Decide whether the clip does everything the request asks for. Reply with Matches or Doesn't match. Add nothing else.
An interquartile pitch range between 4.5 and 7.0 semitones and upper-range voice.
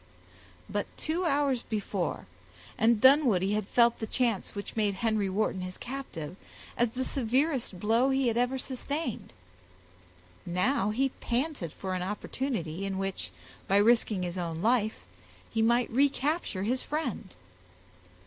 Matches